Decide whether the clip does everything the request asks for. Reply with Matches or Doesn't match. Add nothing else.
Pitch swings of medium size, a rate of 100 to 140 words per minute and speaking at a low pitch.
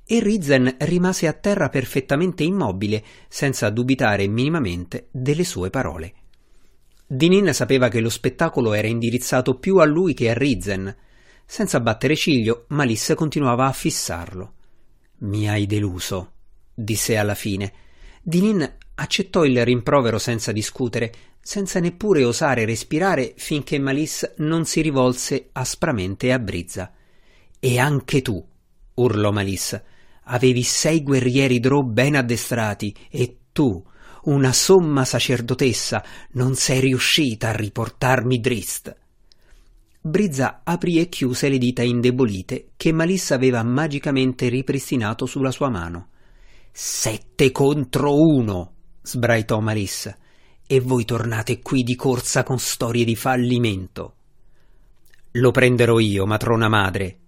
Matches